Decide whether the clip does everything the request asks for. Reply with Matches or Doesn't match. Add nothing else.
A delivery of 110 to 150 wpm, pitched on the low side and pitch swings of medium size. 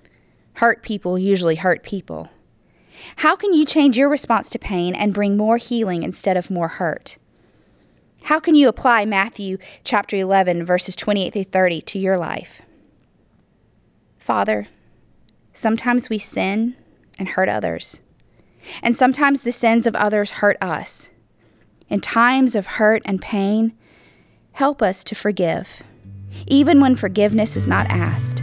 Doesn't match